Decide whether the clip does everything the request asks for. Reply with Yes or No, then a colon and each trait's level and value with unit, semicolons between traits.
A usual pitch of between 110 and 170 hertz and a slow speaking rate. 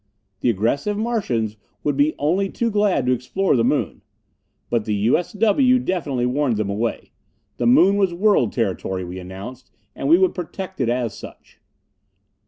No: medium, 140 Hz; average, 160 wpm